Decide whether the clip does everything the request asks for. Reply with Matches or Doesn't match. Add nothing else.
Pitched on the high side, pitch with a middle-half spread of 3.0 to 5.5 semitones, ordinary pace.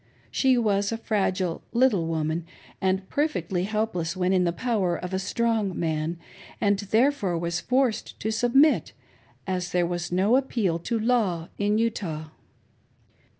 Matches